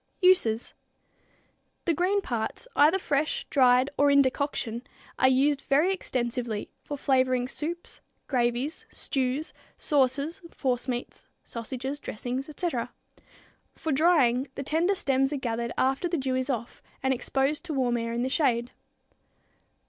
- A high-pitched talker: Yes, very high, 265 Hz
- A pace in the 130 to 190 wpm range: Yes, slow, 135 wpm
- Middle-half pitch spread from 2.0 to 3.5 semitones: Yes, average, 3.2 semitones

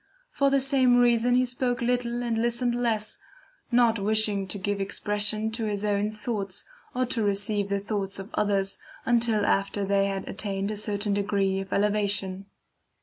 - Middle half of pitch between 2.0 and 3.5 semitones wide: Yes, average, 3.1 semitones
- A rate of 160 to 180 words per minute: Yes, average, 165 wpm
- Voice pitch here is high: Yes, high, 210 Hz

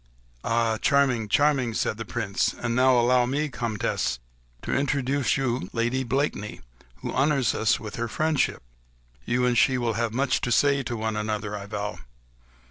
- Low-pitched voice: Yes, low, 120 Hz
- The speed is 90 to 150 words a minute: No, average, 165 wpm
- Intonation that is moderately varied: Yes, average, 3.3 semitones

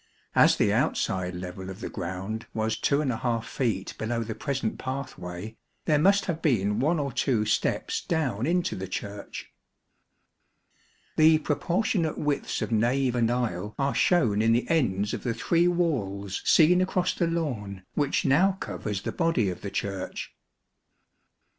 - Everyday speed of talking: Yes, average, 150 wpm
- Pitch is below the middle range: Yes, low, 120 Hz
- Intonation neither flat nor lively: No, wide, 7.3 semitones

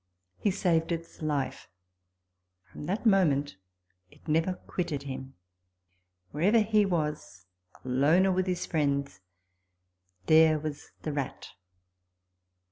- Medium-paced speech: No, slow, 115 wpm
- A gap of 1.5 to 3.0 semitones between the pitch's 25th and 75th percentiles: No, average, 4.4 semitones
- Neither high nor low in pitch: Yes, medium, 155 Hz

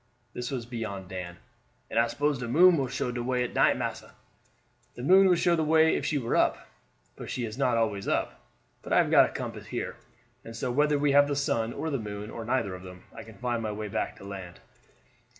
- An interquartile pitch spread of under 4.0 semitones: No, average, 4.9 semitones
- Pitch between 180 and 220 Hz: No, low, 120 Hz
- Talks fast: Yes, fast, 240 wpm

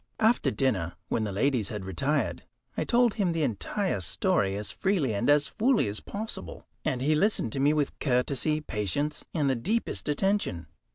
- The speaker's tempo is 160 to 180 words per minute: Yes, average, 175 wpm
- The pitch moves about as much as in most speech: No, wide, 8.7 semitones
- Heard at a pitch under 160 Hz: Yes, medium, 140 Hz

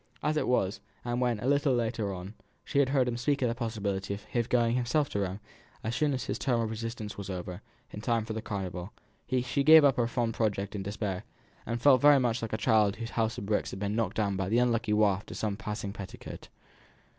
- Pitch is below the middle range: Yes, low, 115 Hz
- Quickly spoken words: Yes, fast, 235 wpm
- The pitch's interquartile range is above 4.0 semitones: No, average, 3.4 semitones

